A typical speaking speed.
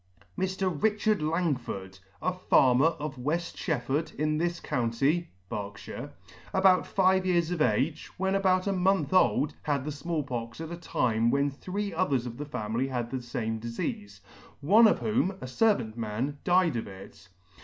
Yes: average, 165 wpm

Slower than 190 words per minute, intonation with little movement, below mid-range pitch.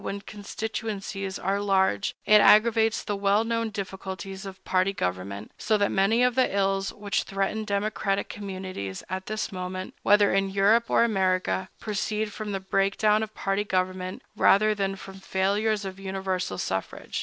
No: average, 160 wpm; narrow, 1.9 semitones; high, 195 Hz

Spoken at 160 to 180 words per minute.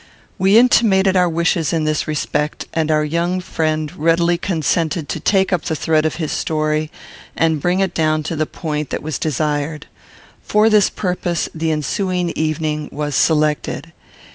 Yes: average, 165 wpm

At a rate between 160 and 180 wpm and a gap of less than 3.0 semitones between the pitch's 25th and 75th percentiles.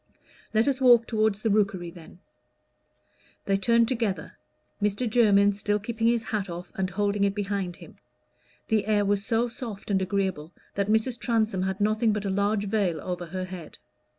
Yes: average, 175 wpm; narrow, 2.6 semitones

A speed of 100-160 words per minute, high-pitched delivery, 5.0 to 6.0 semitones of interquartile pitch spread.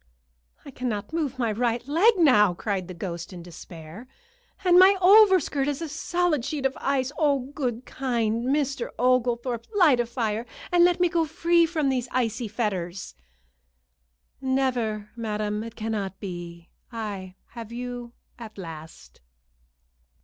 Yes: average, 140 wpm; high, 240 Hz; wide, 5.4 semitones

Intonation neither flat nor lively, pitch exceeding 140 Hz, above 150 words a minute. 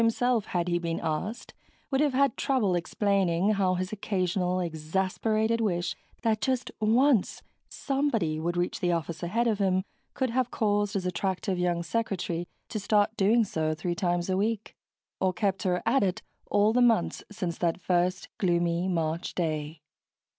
Yes: average, 4.1 semitones; high, 190 Hz; average, 160 wpm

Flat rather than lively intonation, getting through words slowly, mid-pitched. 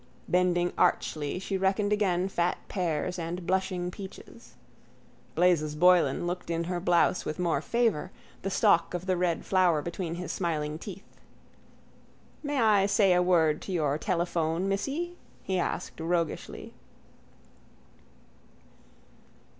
Yes: narrow, 2.2 semitones; slow, 125 wpm; medium, 180 Hz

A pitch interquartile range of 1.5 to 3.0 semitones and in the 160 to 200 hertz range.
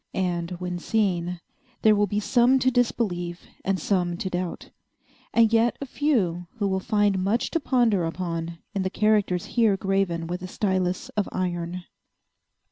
No: average, 3.5 semitones; high, 190 Hz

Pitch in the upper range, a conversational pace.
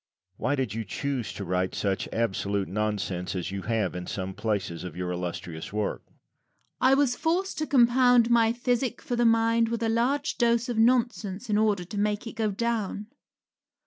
Yes: high, 205 Hz; average, 185 wpm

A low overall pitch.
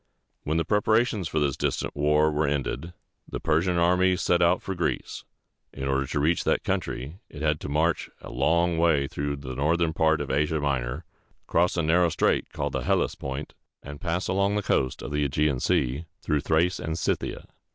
Yes: very low, 80 Hz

